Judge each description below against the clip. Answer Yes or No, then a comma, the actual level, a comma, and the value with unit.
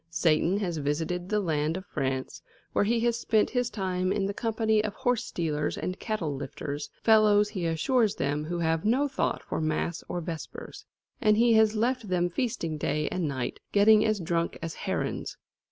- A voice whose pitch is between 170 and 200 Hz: Yes, medium, 185 Hz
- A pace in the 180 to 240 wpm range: Yes, average, 185 wpm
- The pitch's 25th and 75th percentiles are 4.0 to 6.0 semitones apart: Yes, average, 5.3 semitones